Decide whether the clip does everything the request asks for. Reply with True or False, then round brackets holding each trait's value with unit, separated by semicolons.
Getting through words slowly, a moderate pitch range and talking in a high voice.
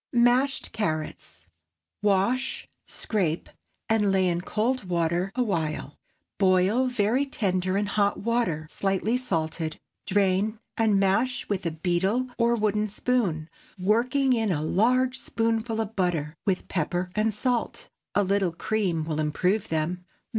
True (130 wpm; 4.4 semitones; 200 Hz)